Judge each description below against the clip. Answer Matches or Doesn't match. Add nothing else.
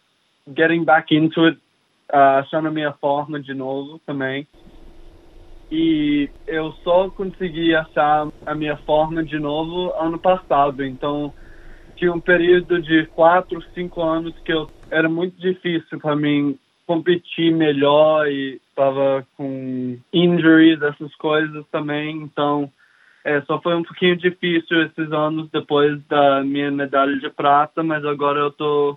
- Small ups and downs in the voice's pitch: Matches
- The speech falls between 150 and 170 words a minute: Doesn't match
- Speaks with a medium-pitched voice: Matches